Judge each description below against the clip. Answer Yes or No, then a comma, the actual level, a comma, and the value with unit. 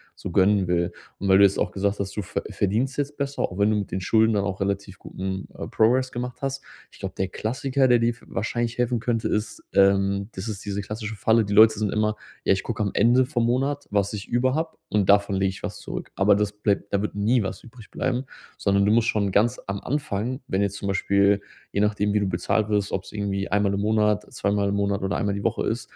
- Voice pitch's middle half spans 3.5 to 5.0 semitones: No, average, 2.7 semitones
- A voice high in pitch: No, low, 105 Hz